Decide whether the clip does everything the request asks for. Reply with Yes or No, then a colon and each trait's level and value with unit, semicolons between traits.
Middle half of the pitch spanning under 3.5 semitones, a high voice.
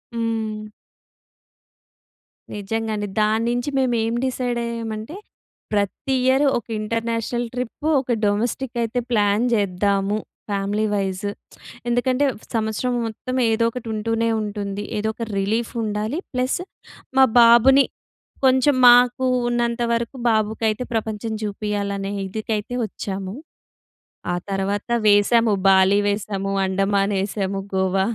Yes: average, 2.8 semitones; high, 220 Hz